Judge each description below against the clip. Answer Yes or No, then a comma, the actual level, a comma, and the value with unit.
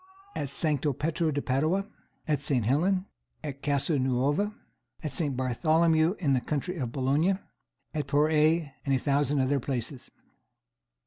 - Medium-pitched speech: Yes, medium, 145 Hz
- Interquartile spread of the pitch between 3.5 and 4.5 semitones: No, average, 2.9 semitones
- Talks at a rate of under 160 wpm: Yes, average, 145 wpm